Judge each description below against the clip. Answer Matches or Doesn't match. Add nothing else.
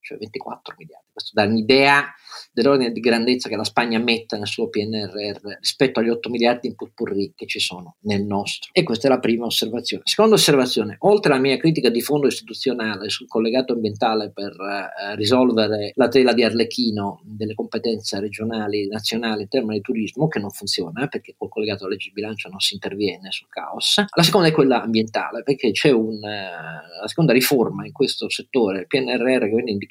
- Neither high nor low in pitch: Doesn't match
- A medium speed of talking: Doesn't match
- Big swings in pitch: Doesn't match